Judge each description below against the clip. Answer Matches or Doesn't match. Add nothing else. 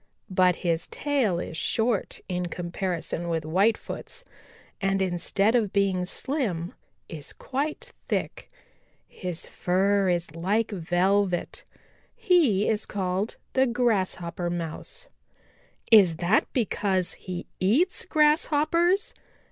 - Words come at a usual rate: Doesn't match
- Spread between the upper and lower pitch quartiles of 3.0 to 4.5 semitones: Doesn't match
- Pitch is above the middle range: Matches